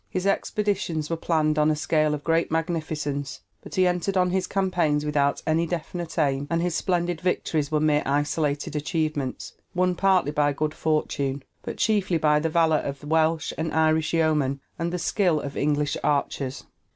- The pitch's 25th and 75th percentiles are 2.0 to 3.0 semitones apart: Yes, average, 2.7 semitones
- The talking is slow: No, average, 175 wpm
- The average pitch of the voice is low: No, medium, 155 Hz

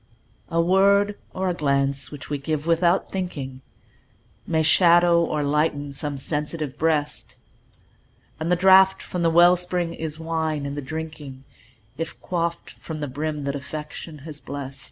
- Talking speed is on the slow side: No, average, 155 wpm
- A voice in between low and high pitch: Yes, medium, 160 Hz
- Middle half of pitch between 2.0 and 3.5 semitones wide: Yes, average, 2.9 semitones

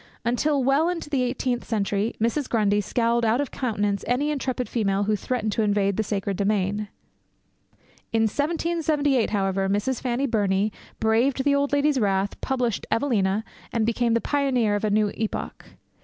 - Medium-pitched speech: No, high, 230 Hz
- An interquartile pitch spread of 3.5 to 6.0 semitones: Yes, average, 4.6 semitones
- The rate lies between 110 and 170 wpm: Yes, average, 160 wpm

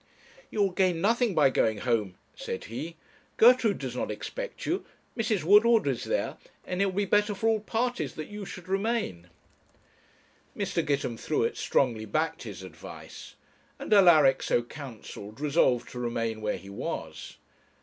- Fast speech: No, average, 155 wpm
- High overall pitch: No, medium, 155 Hz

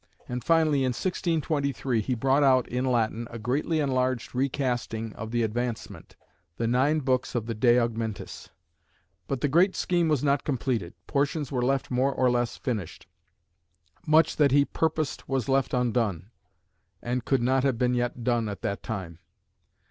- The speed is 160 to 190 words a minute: Yes, average, 165 wpm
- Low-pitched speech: Yes, low, 125 Hz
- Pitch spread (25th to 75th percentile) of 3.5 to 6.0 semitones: No, average, 3.0 semitones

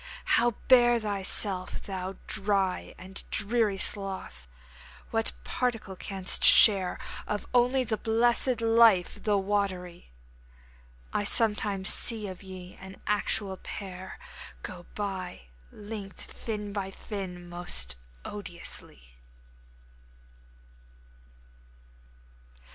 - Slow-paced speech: Yes, slow, 90 wpm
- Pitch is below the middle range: No, high, 200 Hz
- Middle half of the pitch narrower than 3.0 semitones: Yes, narrow, 2.6 semitones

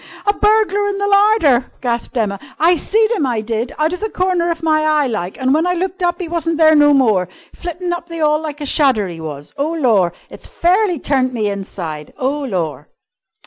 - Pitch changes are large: Yes, wide, 7.1 semitones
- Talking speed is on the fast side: Yes, fast, 215 wpm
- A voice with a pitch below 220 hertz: No, very high, 305 Hz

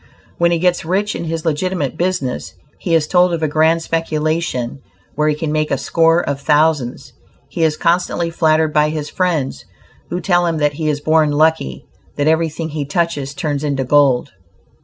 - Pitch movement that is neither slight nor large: No, narrow, 2.2 semitones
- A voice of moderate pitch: Yes, medium, 155 Hz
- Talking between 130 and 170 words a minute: No, average, 180 wpm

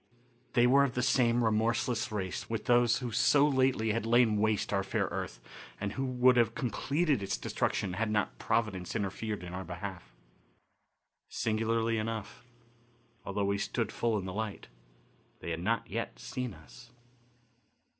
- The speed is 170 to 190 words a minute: No, average, 155 wpm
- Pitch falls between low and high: No, low, 110 Hz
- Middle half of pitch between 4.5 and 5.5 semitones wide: No, average, 3.3 semitones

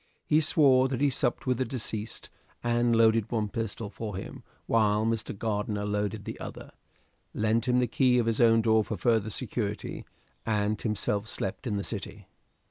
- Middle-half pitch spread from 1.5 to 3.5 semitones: Yes, narrow, 2.4 semitones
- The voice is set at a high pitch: No, low, 110 Hz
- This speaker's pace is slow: No, average, 175 wpm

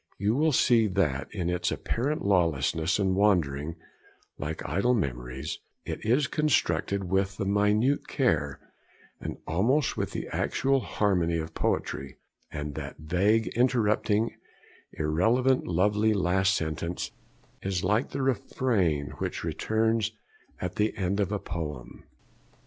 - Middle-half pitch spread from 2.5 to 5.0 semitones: No, wide, 5.4 semitones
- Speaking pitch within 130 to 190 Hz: No, low, 100 Hz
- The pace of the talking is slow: Yes, slow, 125 wpm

